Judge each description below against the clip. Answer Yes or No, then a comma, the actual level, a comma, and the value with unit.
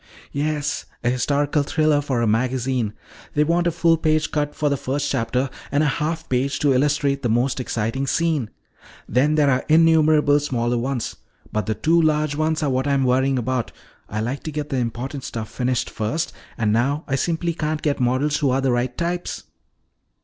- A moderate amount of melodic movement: Yes, average, 3.4 semitones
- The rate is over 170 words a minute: Yes, average, 185 wpm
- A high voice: No, medium, 140 Hz